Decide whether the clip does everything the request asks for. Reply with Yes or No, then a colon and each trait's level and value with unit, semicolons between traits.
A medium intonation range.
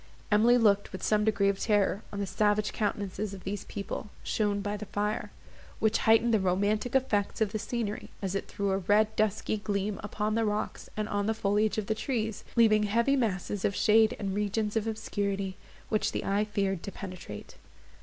No: narrow, 1.5 semitones